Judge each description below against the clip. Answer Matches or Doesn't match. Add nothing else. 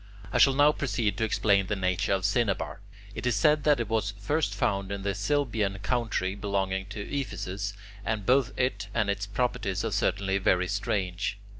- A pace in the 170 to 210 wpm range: Matches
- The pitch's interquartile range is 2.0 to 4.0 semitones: Matches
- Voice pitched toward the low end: Matches